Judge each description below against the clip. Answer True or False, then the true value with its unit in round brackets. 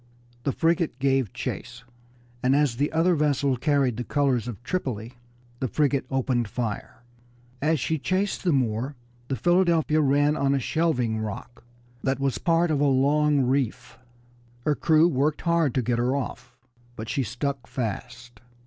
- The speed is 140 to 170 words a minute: True (160 wpm)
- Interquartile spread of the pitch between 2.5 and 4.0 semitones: True (3.6 semitones)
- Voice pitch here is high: False (135 Hz)